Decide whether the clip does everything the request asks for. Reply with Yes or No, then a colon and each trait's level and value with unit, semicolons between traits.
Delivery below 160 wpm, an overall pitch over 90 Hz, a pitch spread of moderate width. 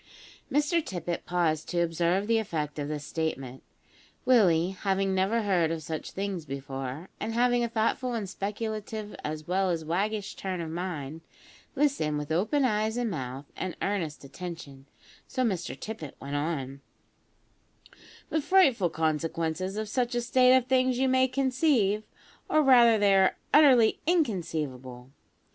No: average, 150 wpm; high, 190 Hz; wide, 6.7 semitones